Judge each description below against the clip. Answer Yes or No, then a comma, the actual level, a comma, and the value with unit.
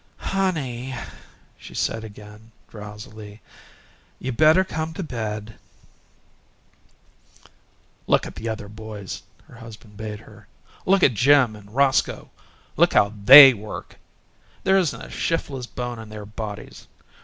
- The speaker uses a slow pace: Yes, slow, 130 wpm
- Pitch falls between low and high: No, low, 115 Hz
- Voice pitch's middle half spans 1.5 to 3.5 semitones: No, average, 4.5 semitones